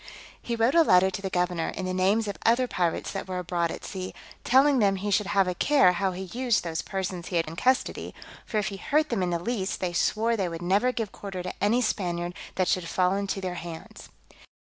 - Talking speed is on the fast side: Yes, fast, 240 wpm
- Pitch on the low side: No, high, 190 Hz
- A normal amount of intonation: Yes, average, 3.6 semitones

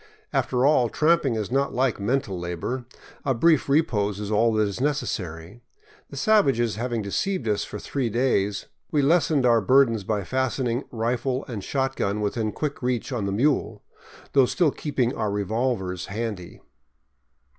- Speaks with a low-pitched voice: Yes, low, 120 Hz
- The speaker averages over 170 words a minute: No, average, 155 wpm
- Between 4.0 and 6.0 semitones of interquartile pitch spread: Yes, average, 4.5 semitones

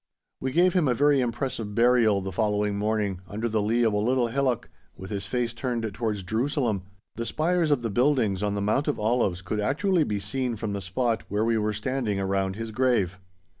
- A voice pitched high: No, low, 110 Hz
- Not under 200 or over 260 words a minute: Yes, fast, 205 wpm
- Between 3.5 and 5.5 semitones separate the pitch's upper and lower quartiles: Yes, average, 3.8 semitones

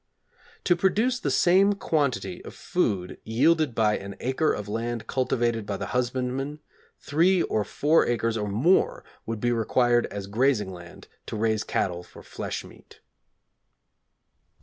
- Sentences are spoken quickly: No, average, 145 wpm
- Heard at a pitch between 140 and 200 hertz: No, low, 120 Hz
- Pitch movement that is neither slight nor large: No, wide, 6.4 semitones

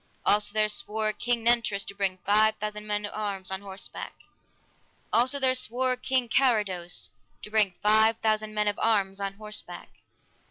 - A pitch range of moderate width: No, narrow, 2.0 semitones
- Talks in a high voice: Yes, high, 215 Hz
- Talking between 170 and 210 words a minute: No, average, 160 wpm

